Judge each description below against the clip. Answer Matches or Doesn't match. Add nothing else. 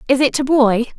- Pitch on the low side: Doesn't match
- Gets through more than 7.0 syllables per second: Doesn't match